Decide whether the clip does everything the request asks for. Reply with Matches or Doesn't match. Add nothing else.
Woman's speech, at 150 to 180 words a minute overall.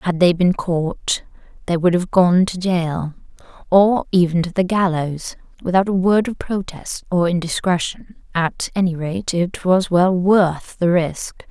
Matches